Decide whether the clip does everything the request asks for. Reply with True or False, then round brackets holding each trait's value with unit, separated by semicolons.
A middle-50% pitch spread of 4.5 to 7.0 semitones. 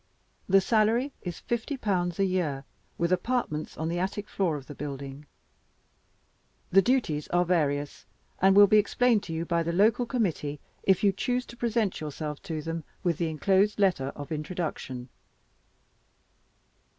True (5.4 semitones)